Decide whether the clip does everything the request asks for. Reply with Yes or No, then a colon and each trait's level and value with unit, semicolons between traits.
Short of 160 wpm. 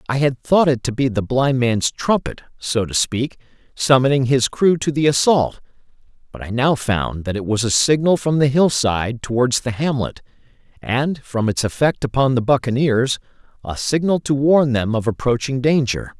No: average, 180 wpm